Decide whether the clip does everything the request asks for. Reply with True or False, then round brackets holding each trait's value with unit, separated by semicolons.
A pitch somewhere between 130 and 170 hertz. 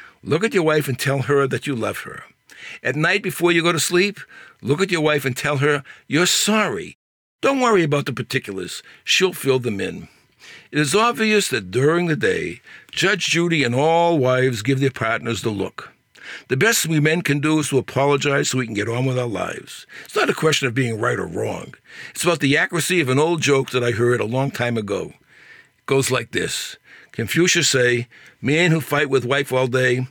True (140 Hz)